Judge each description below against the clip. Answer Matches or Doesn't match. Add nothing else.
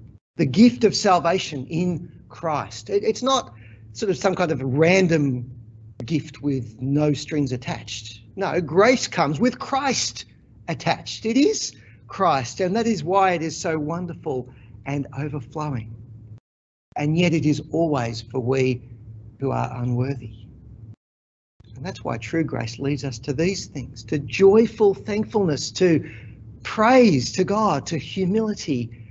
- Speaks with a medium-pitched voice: Matches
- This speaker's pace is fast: Doesn't match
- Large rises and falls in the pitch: Matches